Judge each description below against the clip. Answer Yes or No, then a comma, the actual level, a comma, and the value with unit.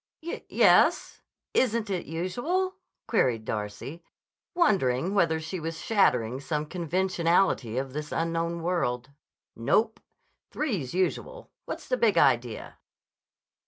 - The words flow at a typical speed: No, slow, 115 wpm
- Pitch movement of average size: No, wide, 7.0 semitones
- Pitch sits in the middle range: Yes, medium, 165 Hz